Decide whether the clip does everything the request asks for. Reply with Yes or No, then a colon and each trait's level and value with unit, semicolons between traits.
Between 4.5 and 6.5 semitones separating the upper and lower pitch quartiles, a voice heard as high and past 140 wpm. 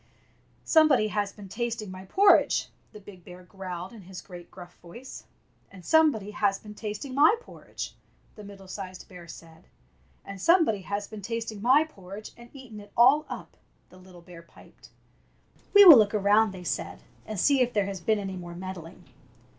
No: average, 4.0 semitones; high, 205 Hz; average, 180 wpm